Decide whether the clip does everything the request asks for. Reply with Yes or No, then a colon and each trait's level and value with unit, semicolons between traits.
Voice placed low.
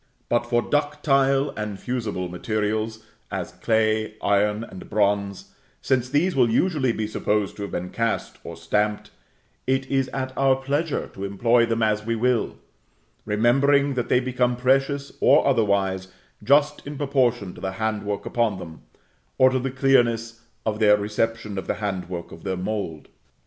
Yes: low, 115 Hz